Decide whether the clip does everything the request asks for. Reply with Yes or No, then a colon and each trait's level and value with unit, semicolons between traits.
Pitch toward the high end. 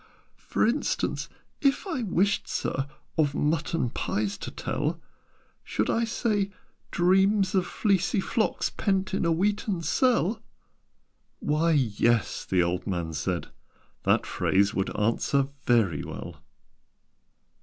No: medium, 165 Hz